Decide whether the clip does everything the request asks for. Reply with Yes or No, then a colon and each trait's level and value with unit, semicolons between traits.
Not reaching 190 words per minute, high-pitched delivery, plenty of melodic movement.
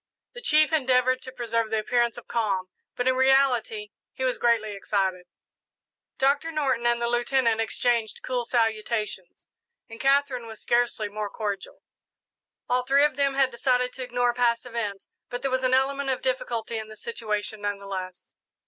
No: average, 170 wpm; high, 240 Hz; average, 3.1 semitones